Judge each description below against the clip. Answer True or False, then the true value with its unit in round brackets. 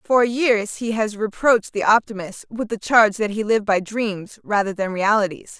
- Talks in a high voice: True (215 Hz)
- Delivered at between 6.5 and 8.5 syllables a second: False (5.0 syllables/s)